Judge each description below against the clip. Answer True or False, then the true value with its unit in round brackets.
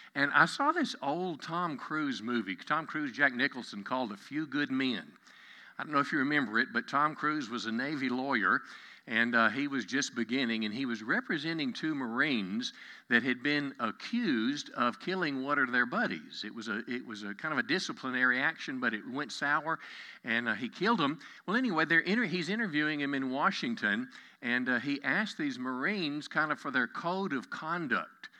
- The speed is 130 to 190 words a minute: False (200 wpm)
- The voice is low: False (150 Hz)